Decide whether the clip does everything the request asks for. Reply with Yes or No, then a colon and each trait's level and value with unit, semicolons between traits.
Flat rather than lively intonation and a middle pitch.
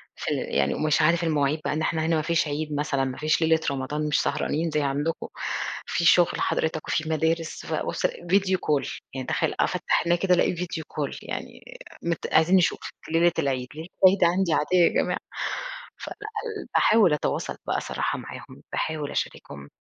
Yes: narrow, 2.3 semitones; medium, 160 Hz